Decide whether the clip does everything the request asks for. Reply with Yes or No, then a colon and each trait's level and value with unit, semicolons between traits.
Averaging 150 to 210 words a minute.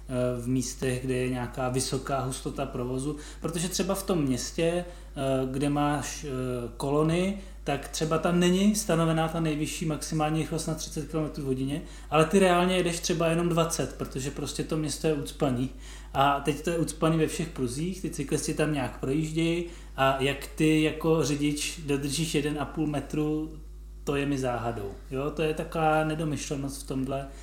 Yes: average, 165 wpm